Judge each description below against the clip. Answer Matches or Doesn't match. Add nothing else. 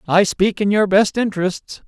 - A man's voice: Matches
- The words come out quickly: Doesn't match